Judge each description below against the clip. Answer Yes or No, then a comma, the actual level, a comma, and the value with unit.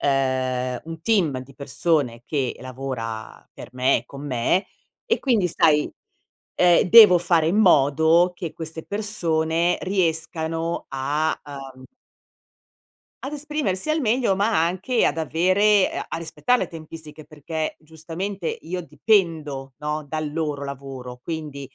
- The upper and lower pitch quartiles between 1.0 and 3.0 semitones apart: No, average, 4.5 semitones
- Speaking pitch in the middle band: Yes, medium, 160 Hz